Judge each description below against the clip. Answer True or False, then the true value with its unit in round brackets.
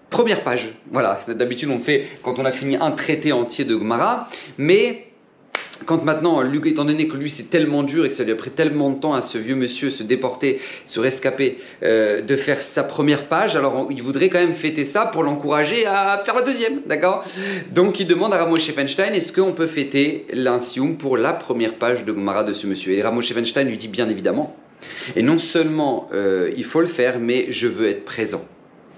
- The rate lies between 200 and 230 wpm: True (215 wpm)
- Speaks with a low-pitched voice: False (145 Hz)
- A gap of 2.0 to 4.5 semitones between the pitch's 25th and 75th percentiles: False (4.9 semitones)